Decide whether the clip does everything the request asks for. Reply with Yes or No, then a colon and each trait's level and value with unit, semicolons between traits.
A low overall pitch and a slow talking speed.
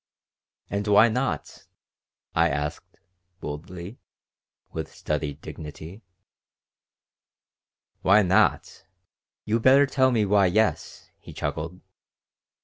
Yes: very low, 95 Hz; slow, 90 wpm